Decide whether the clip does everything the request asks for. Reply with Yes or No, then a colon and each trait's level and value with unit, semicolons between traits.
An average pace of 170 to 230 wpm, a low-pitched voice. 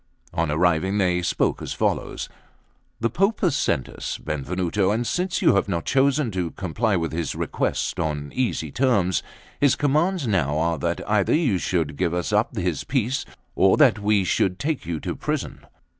Yes: average, 175 wpm; very low, 95 Hz